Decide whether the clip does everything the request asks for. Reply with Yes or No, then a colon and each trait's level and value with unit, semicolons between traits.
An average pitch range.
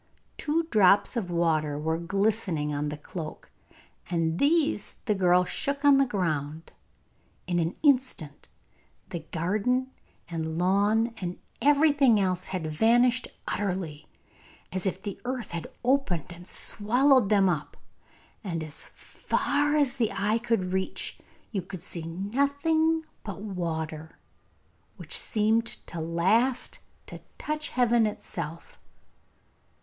No: wide, 6.6 semitones